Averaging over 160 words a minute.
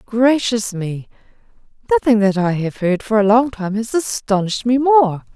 No: average, 155 wpm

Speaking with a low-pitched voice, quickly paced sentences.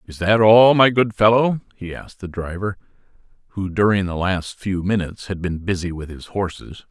No: low, 100 Hz; average, 190 wpm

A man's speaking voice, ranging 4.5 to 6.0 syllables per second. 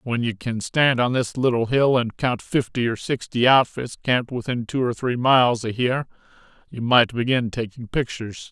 Yes: male; 5.0 syllables/s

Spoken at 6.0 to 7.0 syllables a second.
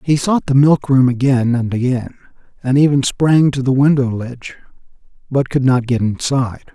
No: 5.0 syllables/s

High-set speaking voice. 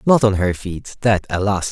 No: low, 100 Hz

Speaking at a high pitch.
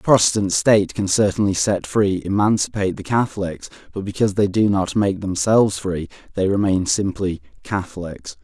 No: very low, 95 Hz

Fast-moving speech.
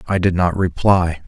No: average, 190 wpm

